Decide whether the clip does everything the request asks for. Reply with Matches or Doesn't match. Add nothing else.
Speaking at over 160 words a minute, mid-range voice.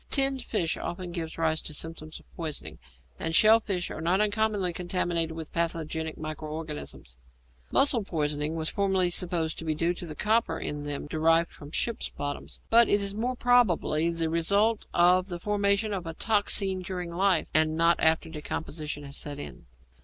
Matches